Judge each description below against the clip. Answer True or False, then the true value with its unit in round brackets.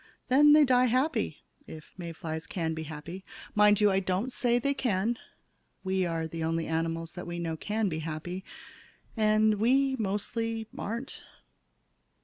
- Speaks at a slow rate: False (155 wpm)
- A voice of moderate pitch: False (195 Hz)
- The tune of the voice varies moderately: False (5.9 semitones)